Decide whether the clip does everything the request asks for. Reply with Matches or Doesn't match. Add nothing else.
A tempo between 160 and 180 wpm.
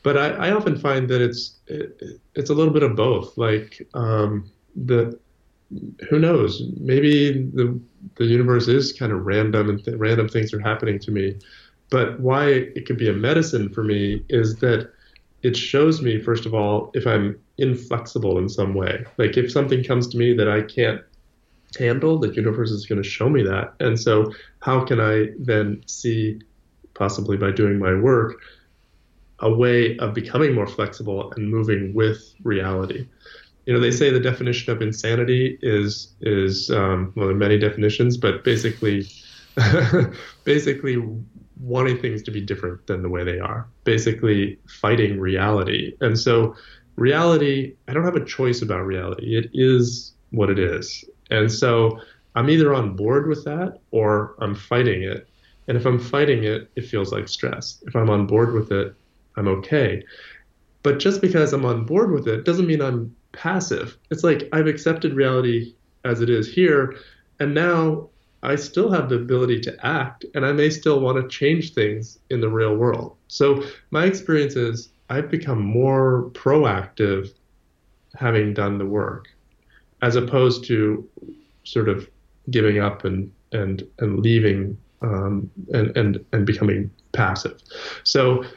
Matches